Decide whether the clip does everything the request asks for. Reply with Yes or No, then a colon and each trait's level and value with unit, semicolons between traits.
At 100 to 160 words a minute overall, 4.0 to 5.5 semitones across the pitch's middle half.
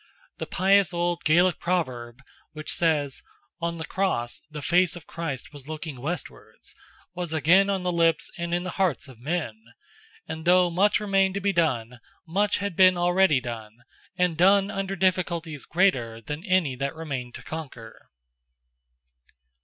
Yes: average, 155 wpm; average, 4.5 semitones